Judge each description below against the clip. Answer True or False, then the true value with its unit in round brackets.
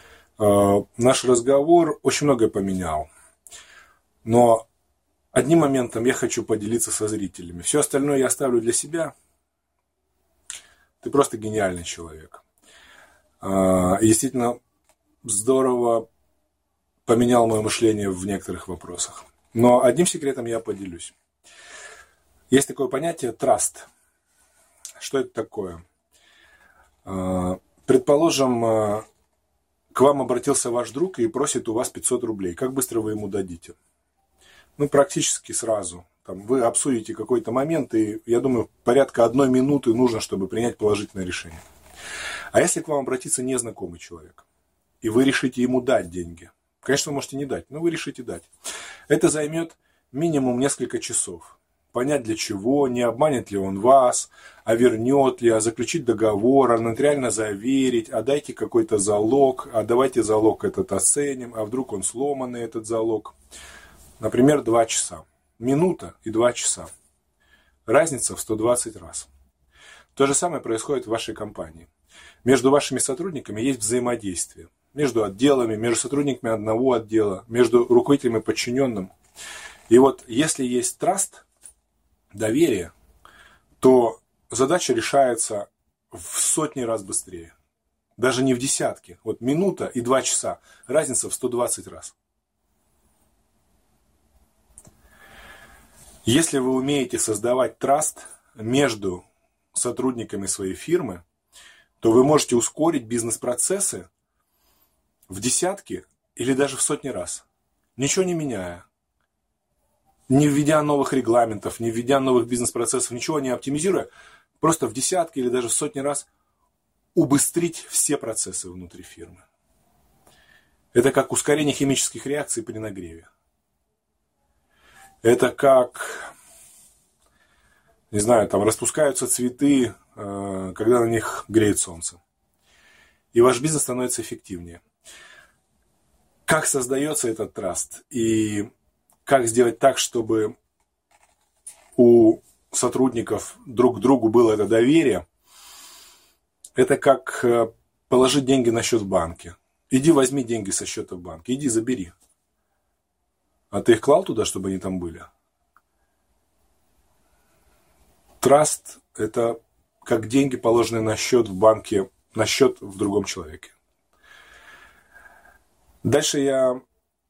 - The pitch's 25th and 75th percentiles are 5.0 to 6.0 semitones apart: True (5.4 semitones)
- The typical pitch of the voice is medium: False (120 Hz)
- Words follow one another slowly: False (120 wpm)